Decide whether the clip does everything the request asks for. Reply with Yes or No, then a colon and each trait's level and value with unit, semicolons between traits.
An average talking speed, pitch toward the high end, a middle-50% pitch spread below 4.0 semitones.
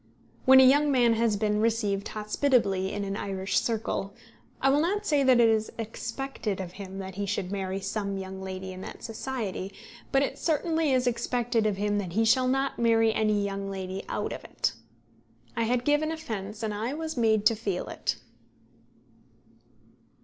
No: average, 180 wpm; high, 220 Hz; average, 4.4 semitones